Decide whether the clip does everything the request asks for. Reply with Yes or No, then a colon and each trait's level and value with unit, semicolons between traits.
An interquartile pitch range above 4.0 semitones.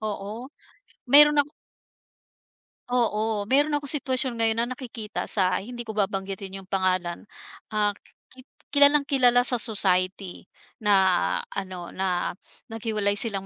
Yes: average, 4.4 semitones